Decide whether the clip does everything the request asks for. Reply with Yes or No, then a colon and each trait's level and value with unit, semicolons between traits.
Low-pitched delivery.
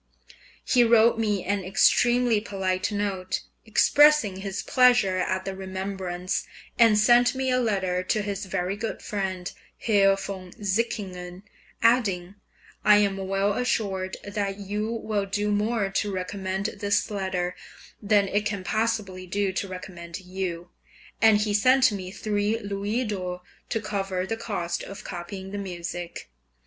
No: high, 200 Hz